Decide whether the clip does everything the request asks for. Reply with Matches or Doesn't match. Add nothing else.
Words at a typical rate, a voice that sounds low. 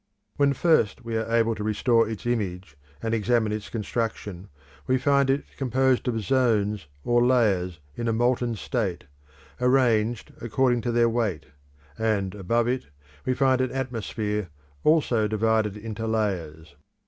Matches